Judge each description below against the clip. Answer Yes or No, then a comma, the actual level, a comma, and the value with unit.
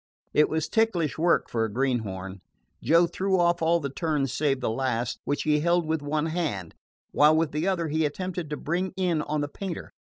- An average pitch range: Yes, average, 3.8 semitones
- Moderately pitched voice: Yes, medium, 155 Hz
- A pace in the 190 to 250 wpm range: Yes, average, 200 wpm